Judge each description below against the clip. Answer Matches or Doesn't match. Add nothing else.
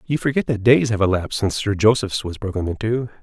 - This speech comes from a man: Matches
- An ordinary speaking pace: Doesn't match